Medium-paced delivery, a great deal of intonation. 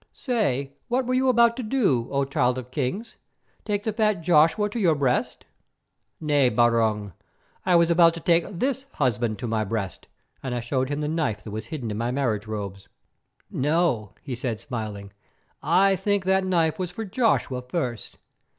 Yes: average, 180 wpm; wide, 8.0 semitones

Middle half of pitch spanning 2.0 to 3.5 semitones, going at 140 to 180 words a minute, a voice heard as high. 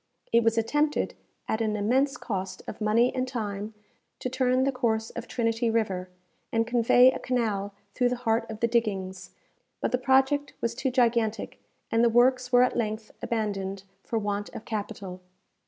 Yes: average, 2.9 semitones; average, 170 wpm; high, 230 Hz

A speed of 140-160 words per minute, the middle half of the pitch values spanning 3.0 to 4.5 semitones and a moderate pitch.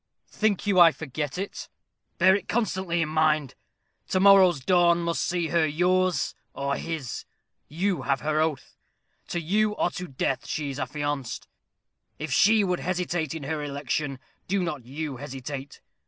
Yes: average, 155 wpm; average, 4.0 semitones; medium, 160 Hz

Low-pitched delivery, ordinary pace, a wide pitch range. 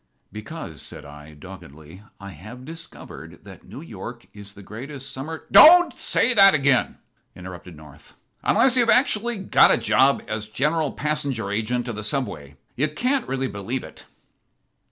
Yes: low, 125 Hz; average, 155 wpm; wide, 7.9 semitones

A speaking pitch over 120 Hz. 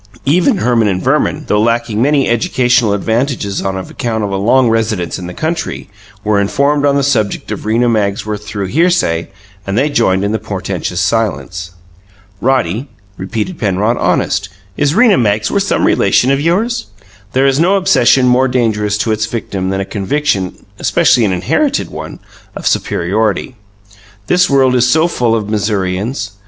No: low, 115 Hz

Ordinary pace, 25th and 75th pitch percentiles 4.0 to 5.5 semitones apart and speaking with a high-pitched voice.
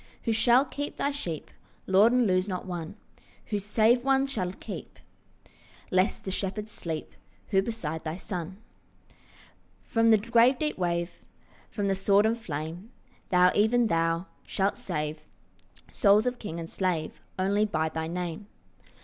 Yes: average, 150 wpm; average, 4.8 semitones; high, 195 Hz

